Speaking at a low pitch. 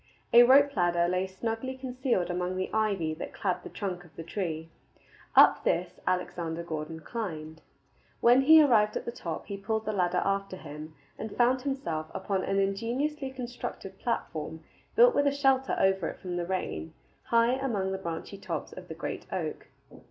No: high, 195 Hz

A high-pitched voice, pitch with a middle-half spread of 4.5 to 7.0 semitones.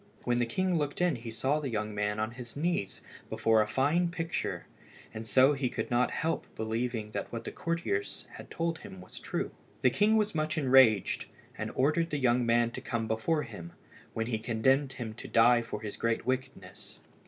No: low, 120 Hz; average, 4.9 semitones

